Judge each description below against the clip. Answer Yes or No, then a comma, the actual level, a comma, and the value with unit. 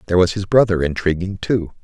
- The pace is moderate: Yes, average, 195 wpm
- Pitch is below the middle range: Yes, very low, 95 Hz